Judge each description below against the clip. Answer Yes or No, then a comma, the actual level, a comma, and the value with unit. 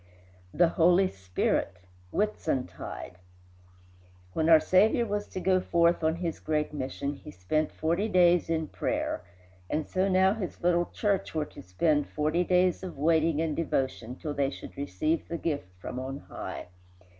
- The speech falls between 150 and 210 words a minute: Yes, average, 160 wpm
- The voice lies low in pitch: No, medium, 160 Hz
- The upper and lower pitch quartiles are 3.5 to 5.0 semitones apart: Yes, average, 3.8 semitones